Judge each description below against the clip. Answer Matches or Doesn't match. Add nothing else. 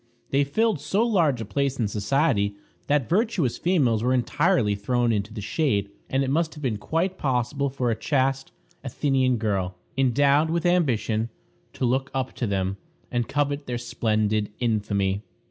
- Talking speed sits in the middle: Matches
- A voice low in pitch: Matches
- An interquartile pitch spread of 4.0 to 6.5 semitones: Matches